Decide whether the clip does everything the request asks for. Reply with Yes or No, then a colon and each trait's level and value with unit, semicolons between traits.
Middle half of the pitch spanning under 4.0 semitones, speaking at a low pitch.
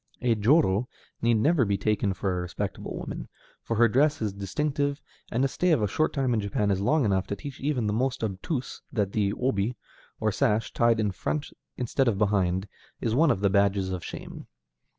No: average, 4.8 semitones; low, 110 Hz